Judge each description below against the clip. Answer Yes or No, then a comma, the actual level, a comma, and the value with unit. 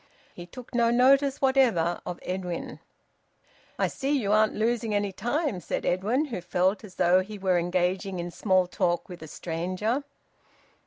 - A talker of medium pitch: No, high, 195 Hz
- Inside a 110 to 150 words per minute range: No, average, 160 wpm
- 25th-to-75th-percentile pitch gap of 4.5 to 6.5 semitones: Yes, average, 5.0 semitones